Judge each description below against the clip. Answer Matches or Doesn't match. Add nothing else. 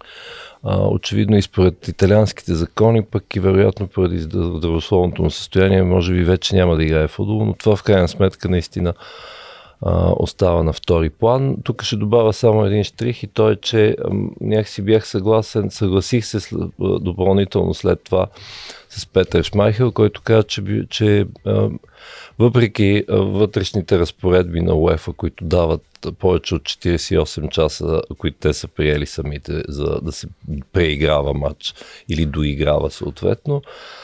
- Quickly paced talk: Doesn't match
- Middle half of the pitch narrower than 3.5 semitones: Doesn't match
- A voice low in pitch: Matches